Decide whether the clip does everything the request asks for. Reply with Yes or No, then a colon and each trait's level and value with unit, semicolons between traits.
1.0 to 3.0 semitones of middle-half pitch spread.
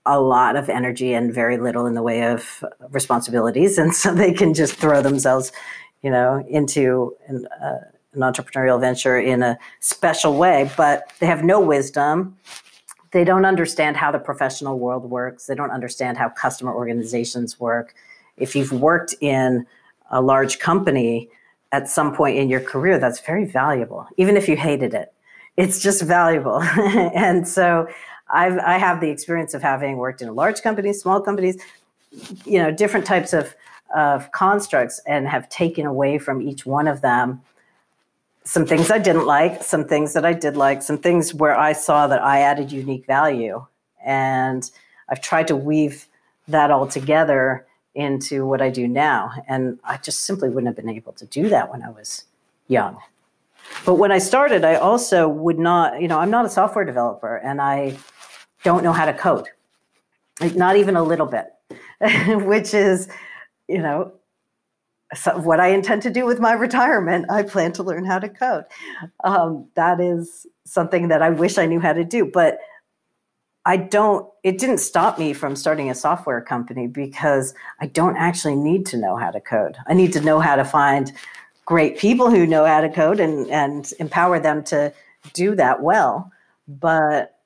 No: average, 5.1 semitones